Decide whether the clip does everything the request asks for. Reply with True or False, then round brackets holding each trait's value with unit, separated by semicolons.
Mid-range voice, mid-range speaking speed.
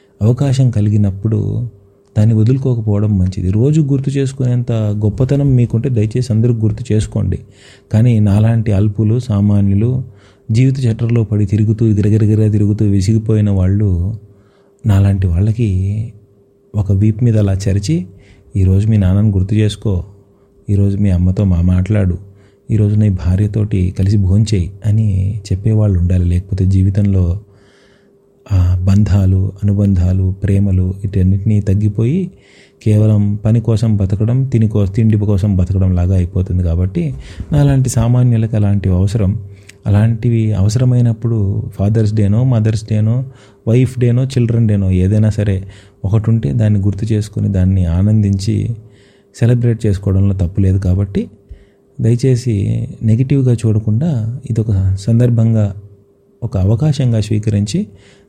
False (105 Hz; 110 wpm)